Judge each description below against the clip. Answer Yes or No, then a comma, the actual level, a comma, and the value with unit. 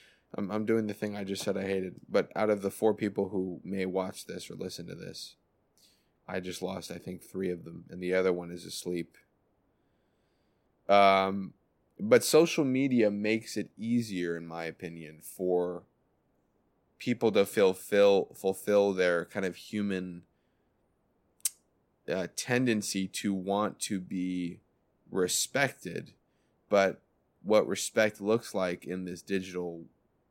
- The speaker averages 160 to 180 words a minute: No, average, 145 wpm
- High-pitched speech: No, very low, 95 Hz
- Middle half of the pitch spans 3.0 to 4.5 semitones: No, narrow, 2.5 semitones